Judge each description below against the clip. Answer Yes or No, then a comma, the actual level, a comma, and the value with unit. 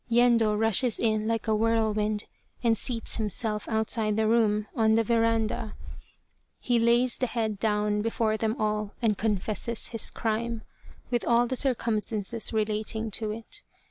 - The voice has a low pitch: No, high, 220 Hz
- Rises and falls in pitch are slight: Yes, narrow, 1.4 semitones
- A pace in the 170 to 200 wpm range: No, average, 145 wpm